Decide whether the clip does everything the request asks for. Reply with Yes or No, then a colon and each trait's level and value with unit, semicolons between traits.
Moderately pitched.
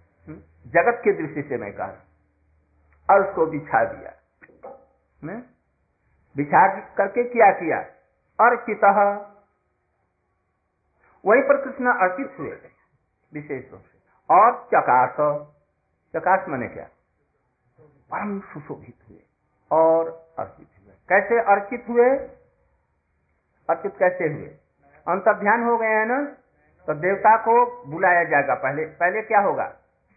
Yes: medium, 160 Hz